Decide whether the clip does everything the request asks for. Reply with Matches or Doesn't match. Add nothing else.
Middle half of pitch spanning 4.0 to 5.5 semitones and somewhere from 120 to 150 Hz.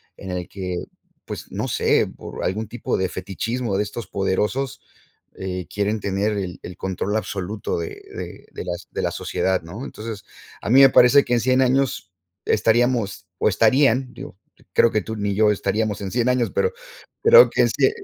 Doesn't match